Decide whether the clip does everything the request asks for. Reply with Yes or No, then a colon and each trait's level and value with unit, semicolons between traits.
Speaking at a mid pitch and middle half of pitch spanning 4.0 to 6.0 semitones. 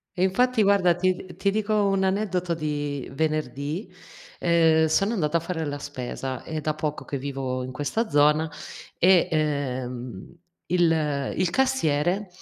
Yes: medium, 160 Hz; average, 4.4 semitones